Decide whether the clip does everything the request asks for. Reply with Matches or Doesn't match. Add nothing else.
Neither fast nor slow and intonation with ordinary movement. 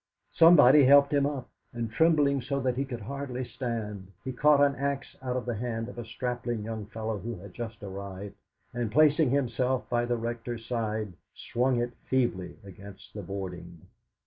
Matches